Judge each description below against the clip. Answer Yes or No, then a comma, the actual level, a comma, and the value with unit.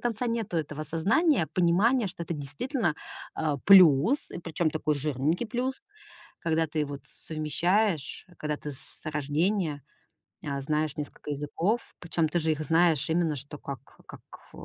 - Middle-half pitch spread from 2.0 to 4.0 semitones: No, average, 4.4 semitones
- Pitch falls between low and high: Yes, medium, 160 Hz